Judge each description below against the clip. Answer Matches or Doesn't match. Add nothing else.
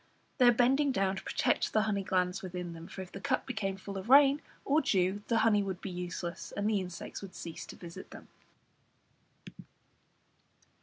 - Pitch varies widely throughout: Doesn't match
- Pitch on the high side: Matches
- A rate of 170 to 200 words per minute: Matches